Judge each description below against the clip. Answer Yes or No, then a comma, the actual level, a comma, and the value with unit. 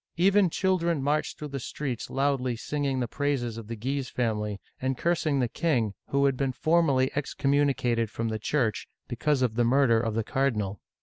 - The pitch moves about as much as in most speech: Yes, average, 3.8 semitones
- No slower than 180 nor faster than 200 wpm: Yes, average, 190 wpm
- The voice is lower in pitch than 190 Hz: Yes, low, 135 Hz